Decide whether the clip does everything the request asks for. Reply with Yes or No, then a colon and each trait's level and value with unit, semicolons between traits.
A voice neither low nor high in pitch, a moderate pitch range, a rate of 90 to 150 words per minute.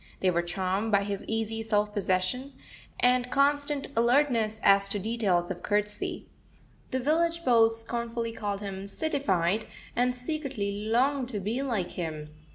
No: high, 225 Hz; average, 4.1 semitones; average, 145 wpm